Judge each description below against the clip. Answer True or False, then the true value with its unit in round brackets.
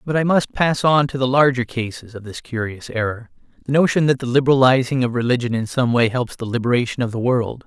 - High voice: False (125 Hz)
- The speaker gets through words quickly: True (225 wpm)